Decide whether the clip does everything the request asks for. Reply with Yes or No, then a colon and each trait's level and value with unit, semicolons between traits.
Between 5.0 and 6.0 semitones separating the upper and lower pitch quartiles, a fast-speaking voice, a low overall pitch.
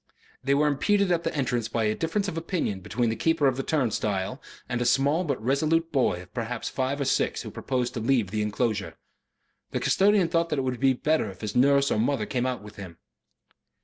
Yes: average, 5.3 semitones; fast, 225 wpm; low, 130 Hz